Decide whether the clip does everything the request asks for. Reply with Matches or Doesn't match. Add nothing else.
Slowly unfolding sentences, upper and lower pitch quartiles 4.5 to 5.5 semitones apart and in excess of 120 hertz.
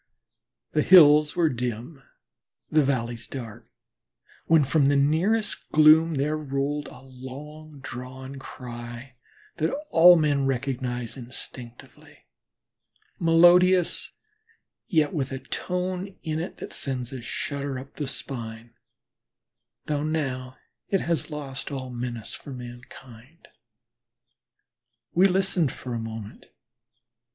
Doesn't match